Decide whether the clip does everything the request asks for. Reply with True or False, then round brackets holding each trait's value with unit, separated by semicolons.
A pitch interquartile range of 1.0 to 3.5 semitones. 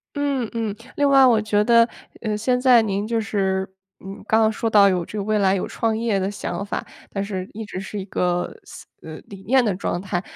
True (2.9 semitones)